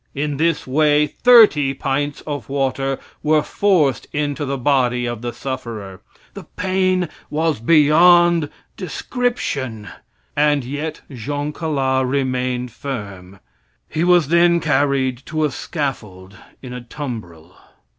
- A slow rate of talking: Yes, slow, 120 wpm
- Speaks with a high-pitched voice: No, medium, 140 Hz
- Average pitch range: Yes, average, 3.6 semitones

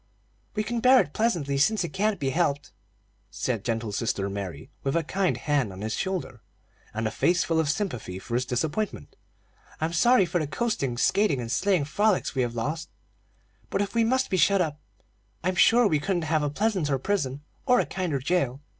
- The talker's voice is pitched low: No, medium, 160 Hz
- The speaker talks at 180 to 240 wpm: Yes, average, 195 wpm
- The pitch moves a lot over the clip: Yes, wide, 7.3 semitones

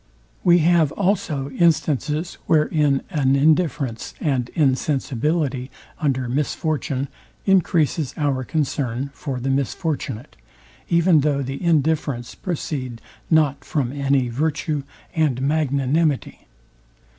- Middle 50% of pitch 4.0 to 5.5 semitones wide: No, average, 2.9 semitones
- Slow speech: Yes, slow, 100 wpm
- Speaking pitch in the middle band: Yes, medium, 145 Hz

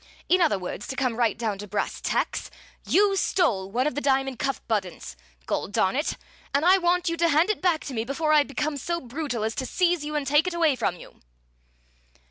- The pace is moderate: No, fast, 225 wpm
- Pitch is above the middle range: Yes, very high, 280 Hz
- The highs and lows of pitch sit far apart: Yes, wide, 6.5 semitones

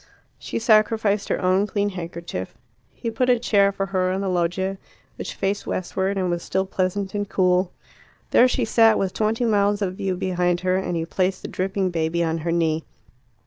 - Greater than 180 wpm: Yes, average, 190 wpm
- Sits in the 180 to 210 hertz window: Yes, high, 190 Hz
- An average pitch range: No, narrow, 2.3 semitones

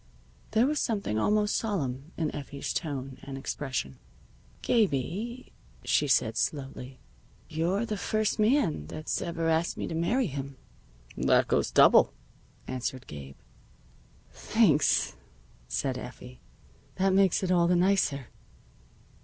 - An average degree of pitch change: No, wide, 6.9 semitones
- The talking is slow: Yes, slow, 120 wpm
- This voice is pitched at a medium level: Yes, medium, 165 Hz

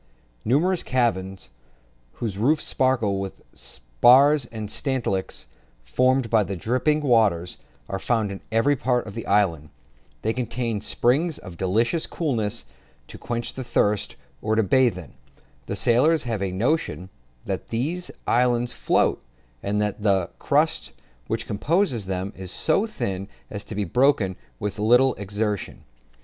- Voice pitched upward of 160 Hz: No, low, 115 Hz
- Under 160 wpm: Yes, average, 145 wpm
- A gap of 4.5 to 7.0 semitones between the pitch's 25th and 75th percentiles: Yes, average, 4.8 semitones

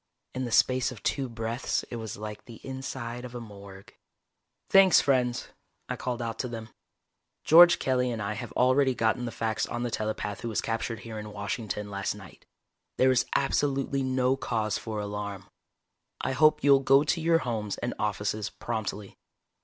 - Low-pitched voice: Yes, low, 120 Hz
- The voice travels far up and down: No, average, 3.6 semitones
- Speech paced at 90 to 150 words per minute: No, average, 175 wpm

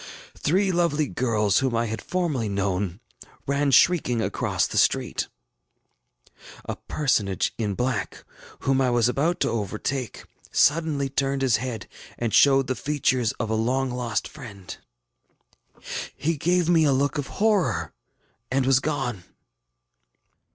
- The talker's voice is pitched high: No, low, 130 Hz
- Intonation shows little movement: No, average, 4.3 semitones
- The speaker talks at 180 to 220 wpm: No, slow, 135 wpm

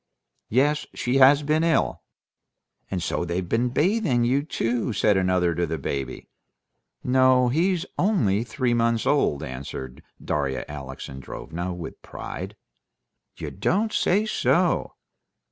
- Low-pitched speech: Yes, low, 120 Hz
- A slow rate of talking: Yes, slow, 125 wpm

